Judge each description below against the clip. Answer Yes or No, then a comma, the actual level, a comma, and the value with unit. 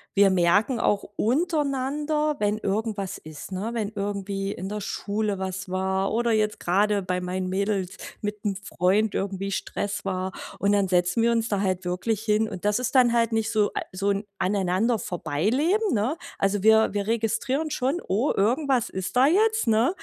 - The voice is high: Yes, high, 205 Hz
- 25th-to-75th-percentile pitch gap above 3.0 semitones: Yes, average, 3.4 semitones